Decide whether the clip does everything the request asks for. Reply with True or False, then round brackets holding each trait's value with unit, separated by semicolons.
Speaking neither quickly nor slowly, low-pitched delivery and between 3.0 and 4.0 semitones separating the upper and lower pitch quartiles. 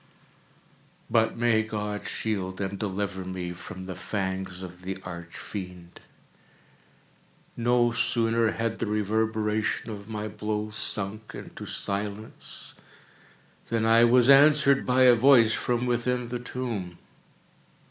False (120 wpm; 110 Hz; 3.6 semitones)